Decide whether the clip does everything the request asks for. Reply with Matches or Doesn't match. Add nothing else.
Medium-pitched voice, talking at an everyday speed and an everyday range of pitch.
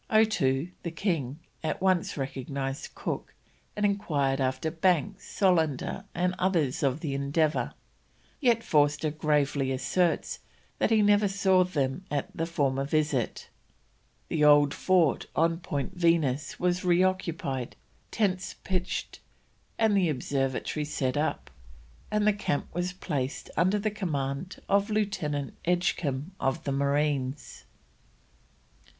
Doesn't match